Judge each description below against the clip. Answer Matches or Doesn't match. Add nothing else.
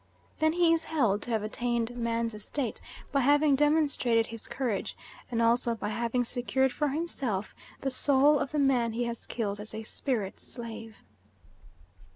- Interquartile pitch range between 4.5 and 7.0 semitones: Doesn't match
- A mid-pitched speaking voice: Doesn't match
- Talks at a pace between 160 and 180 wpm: Matches